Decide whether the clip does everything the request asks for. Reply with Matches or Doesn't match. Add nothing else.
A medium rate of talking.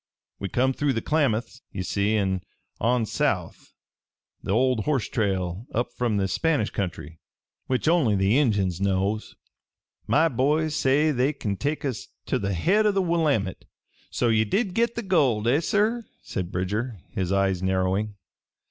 Matches